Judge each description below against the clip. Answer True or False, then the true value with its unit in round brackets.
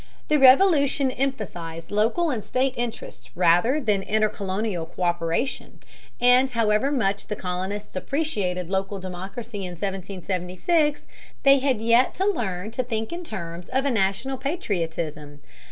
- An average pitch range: False (6.2 semitones)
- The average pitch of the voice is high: True (215 Hz)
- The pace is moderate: False (130 wpm)